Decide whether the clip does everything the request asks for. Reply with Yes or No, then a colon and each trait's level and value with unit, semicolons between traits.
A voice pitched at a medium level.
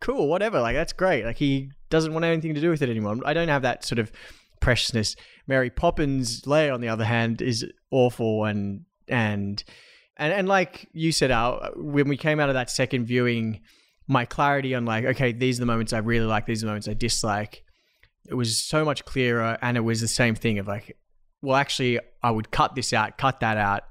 No: low, 120 Hz